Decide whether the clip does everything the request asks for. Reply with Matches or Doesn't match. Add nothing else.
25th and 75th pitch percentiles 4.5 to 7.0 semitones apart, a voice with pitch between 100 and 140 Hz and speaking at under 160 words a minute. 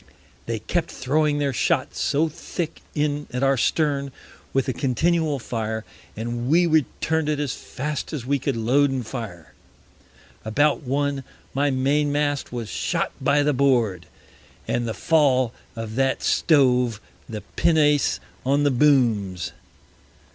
Doesn't match